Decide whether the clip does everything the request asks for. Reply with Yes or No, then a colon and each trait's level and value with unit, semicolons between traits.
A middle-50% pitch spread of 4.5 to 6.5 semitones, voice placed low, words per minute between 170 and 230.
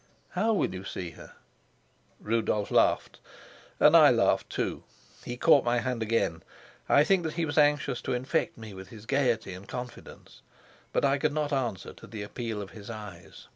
Yes: wide, 5.6 semitones; low, 120 Hz; average, 180 wpm